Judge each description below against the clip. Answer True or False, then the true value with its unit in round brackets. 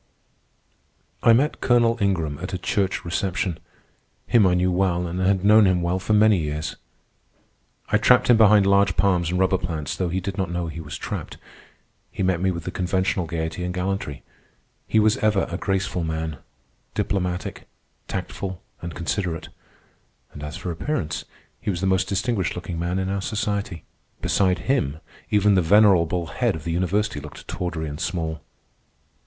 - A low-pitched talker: True (90 Hz)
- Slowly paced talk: False (170 wpm)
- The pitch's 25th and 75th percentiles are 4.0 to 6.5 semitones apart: False (2.8 semitones)